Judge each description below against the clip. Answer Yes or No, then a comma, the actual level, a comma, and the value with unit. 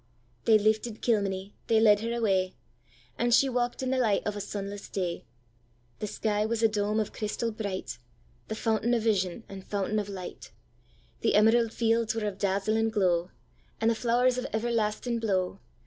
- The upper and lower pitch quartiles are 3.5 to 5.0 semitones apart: No, average, 3.0 semitones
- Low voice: No, high, 210 Hz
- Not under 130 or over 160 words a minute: Yes, average, 155 wpm